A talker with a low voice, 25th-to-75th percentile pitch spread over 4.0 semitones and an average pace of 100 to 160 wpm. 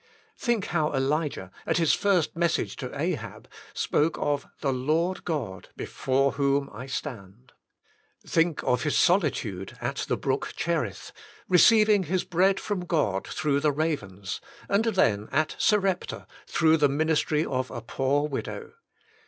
No: medium, 150 Hz; average, 4.7 semitones; average, 145 wpm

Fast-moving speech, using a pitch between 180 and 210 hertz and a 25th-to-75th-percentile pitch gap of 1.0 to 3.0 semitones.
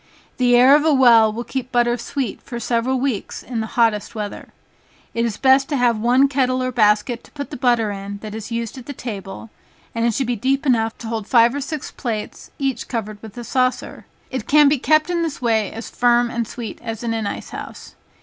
No: fast, 225 wpm; high, 240 Hz; average, 2.7 semitones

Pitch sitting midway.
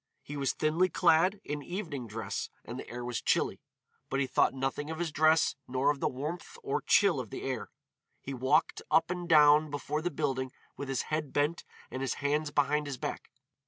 Yes: medium, 145 Hz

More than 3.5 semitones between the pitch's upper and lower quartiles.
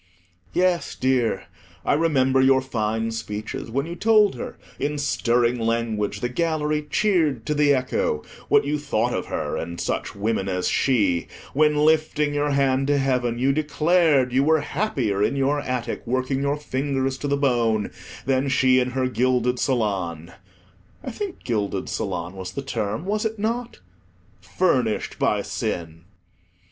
Yes: average, 4.7 semitones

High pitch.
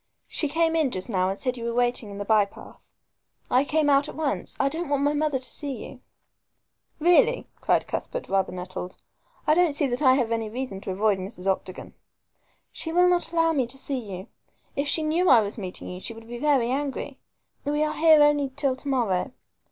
Yes: very high, 265 Hz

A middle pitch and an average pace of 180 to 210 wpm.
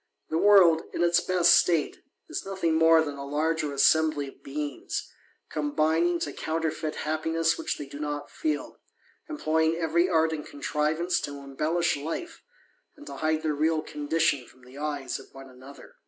No: medium, 155 Hz; average, 165 wpm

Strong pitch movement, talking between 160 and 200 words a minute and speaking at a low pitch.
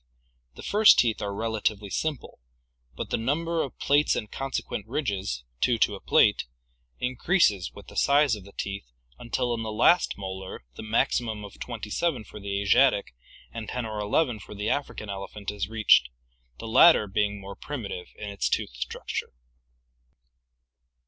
No: average, 3.9 semitones; average, 170 wpm; low, 110 Hz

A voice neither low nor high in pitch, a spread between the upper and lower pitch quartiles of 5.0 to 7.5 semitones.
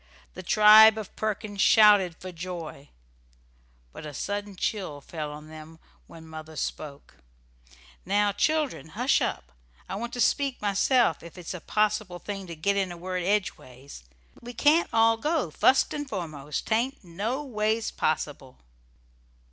No: high, 195 Hz; average, 5.3 semitones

